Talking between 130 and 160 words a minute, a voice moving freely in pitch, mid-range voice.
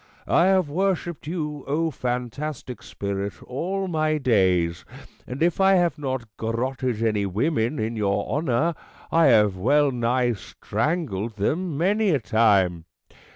No: average, 140 wpm; wide, 6.6 semitones; low, 130 Hz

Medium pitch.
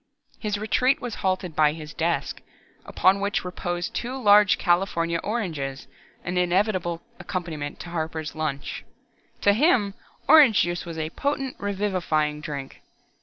Yes: medium, 180 Hz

